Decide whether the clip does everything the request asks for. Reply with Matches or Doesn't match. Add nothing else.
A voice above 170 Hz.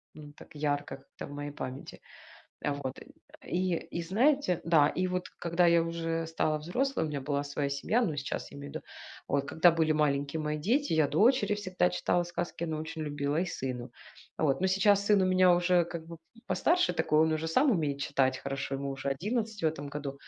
Doesn't match